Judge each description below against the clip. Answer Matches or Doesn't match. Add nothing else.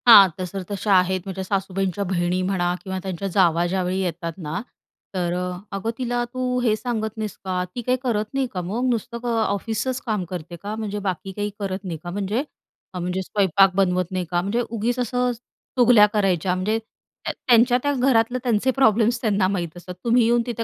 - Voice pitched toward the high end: Matches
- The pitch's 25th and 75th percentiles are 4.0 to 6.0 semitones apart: Matches